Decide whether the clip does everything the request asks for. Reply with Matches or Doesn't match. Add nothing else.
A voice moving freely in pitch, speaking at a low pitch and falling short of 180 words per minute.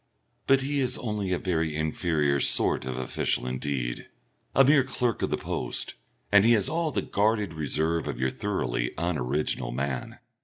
Matches